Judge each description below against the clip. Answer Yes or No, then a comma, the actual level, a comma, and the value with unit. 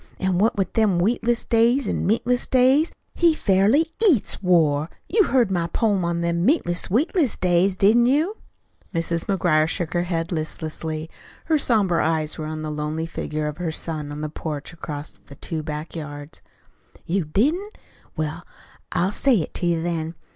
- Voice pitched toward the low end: No, medium, 175 Hz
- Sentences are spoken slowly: No, average, 170 wpm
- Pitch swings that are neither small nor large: No, wide, 6.3 semitones